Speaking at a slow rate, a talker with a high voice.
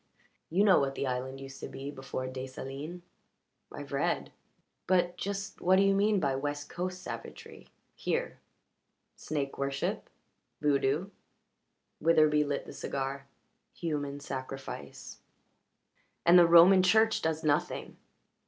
No: slow, 125 wpm; medium, 150 Hz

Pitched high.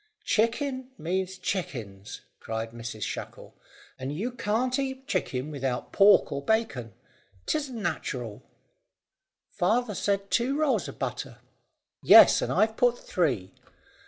Yes: high, 195 Hz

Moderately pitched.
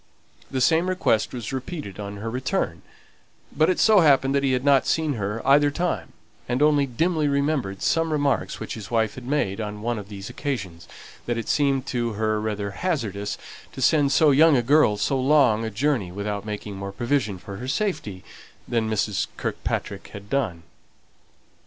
No: low, 125 Hz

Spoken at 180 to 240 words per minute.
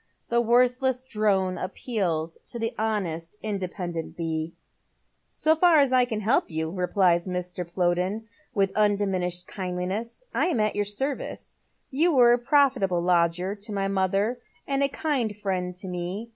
No: average, 160 wpm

